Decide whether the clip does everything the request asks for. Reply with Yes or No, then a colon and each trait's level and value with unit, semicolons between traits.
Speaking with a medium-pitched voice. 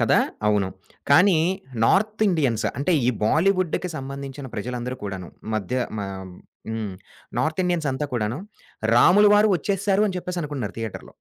Yes: medium, 145 Hz